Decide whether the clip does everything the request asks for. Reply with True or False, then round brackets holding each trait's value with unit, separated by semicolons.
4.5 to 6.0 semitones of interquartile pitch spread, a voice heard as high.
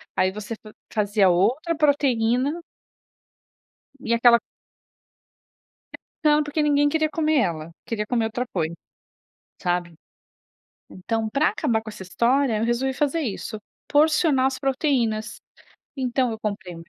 True (5.4 semitones; 240 Hz)